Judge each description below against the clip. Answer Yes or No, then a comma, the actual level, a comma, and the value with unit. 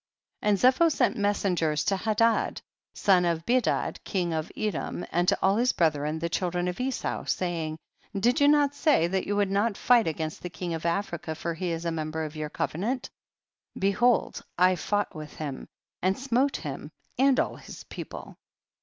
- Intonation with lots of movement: Yes, wide, 5.7 semitones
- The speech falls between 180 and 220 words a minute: Yes, average, 190 wpm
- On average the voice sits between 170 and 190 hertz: Yes, medium, 185 Hz